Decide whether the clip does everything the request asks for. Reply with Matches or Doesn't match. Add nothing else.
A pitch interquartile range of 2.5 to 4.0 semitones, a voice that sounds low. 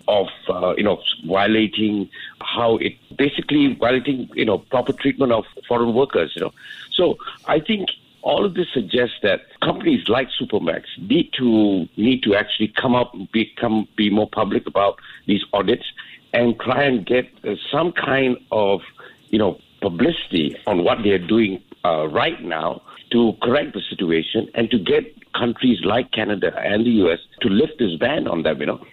Matches